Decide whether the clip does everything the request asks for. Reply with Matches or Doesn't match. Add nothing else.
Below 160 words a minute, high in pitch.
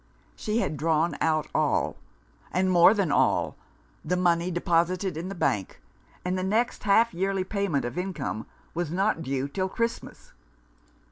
Doesn't match